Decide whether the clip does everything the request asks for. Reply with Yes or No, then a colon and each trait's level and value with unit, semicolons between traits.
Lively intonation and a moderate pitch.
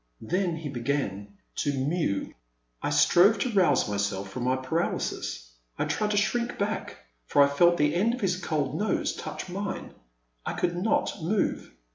Yes: wide, 7.4 semitones; medium, 160 Hz